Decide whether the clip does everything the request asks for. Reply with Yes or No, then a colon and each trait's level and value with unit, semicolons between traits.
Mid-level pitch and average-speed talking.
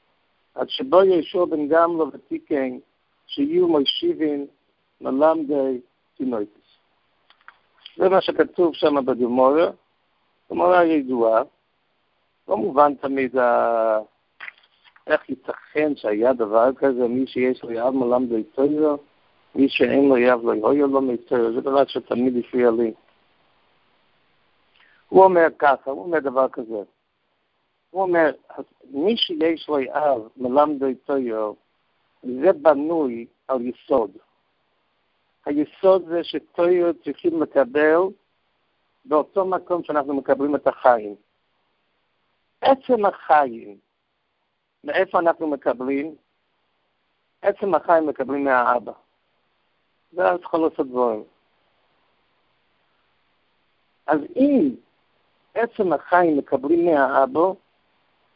No: medium, 145 Hz; slow, 100 wpm